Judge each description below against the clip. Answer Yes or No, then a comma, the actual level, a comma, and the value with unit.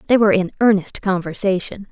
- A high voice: Yes, high, 195 Hz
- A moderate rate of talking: Yes, average, 155 wpm